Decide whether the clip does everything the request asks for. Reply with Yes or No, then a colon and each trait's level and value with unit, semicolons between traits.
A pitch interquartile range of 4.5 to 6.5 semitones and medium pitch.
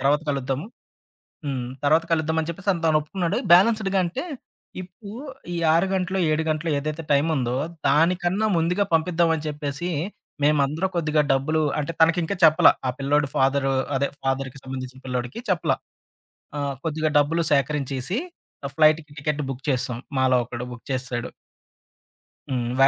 No: average, 3.6 semitones; medium, 150 Hz